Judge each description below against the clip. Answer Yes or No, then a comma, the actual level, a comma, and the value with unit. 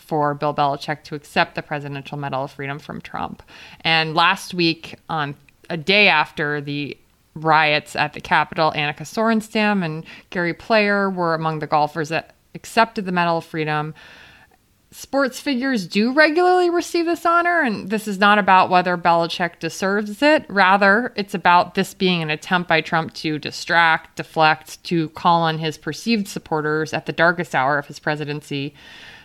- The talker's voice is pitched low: No, medium, 165 Hz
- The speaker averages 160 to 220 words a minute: Yes, average, 165 wpm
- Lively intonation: No, average, 4.7 semitones